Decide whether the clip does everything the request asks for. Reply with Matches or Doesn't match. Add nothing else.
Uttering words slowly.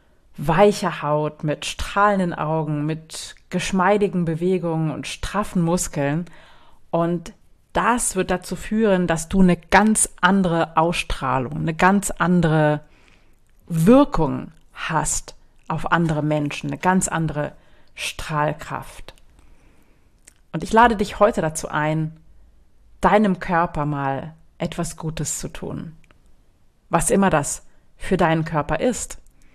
Matches